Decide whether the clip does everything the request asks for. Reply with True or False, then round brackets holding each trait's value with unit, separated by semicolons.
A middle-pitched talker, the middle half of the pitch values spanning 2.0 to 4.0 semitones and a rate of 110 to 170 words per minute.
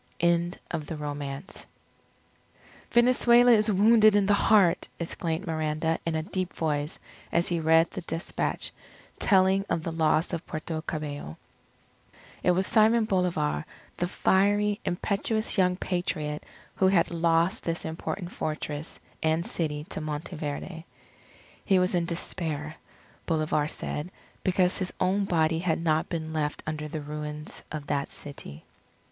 True (165 Hz; 3.4 semitones; 140 wpm)